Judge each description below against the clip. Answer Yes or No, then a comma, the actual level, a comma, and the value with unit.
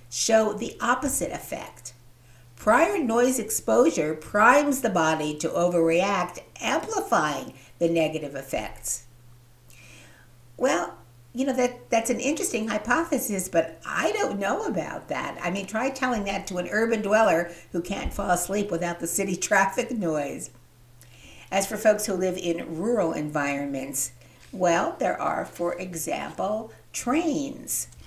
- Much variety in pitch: Yes, wide, 8.2 semitones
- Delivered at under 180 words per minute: Yes, slow, 135 wpm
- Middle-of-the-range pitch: Yes, medium, 175 Hz